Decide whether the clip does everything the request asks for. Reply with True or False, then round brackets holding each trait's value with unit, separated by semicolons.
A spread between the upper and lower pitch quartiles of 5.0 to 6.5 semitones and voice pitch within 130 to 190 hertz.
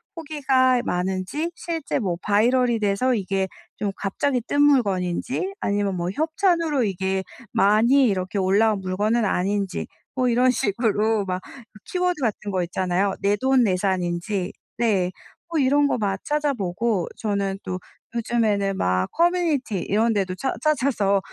False (5.3 semitones; 210 Hz)